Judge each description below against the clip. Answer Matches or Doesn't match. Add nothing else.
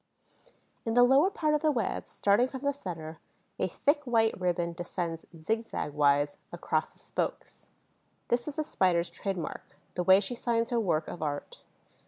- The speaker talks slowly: Doesn't match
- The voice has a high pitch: Matches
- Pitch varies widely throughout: Matches